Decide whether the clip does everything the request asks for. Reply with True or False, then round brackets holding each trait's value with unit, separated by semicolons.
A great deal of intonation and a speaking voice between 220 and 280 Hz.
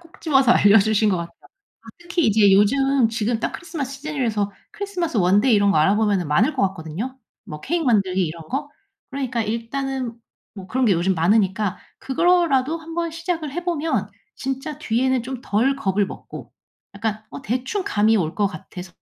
True (5.7 semitones; 230 Hz)